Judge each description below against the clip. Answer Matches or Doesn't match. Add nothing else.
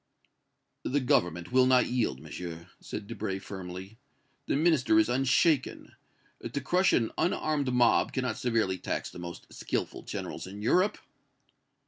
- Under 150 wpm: Matches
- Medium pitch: Doesn't match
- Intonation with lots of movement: Matches